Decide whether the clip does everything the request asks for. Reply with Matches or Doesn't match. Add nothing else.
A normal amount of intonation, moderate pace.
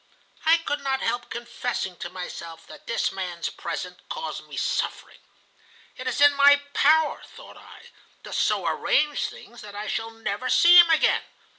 Doesn't match